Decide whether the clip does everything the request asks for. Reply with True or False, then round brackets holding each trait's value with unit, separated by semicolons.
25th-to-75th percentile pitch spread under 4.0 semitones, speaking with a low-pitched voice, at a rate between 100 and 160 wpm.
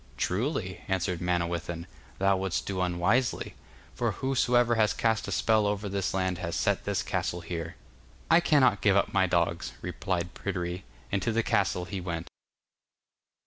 True (3.4 semitones; 95 Hz; 155 wpm)